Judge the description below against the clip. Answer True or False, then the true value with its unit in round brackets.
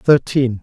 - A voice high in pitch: False (130 Hz)